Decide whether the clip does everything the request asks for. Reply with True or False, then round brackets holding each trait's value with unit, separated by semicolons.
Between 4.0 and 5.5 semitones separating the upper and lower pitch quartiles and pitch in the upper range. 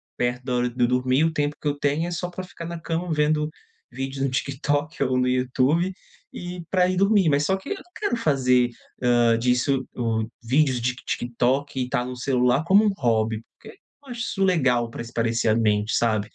False (5.0 semitones; 135 Hz)